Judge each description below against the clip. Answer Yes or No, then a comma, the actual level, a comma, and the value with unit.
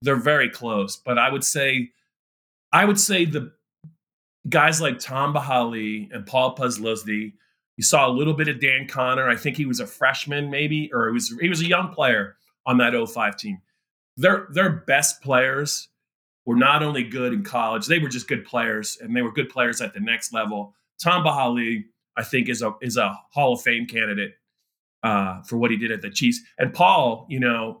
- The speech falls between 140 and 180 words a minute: No, average, 200 wpm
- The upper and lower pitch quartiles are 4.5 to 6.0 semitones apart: Yes, average, 4.8 semitones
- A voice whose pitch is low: Yes, low, 130 Hz